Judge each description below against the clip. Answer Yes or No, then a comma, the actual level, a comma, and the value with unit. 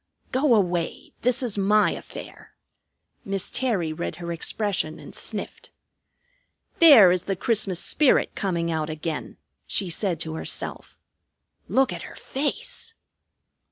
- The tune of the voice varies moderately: No, wide, 6.6 semitones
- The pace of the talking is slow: Yes, slow, 125 wpm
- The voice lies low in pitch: No, high, 195 Hz